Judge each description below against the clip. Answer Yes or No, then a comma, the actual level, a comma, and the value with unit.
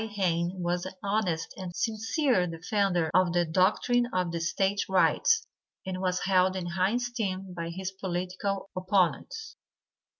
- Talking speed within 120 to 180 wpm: Yes, average, 140 wpm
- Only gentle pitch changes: Yes, narrow, 2.3 semitones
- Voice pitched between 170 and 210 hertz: Yes, medium, 185 Hz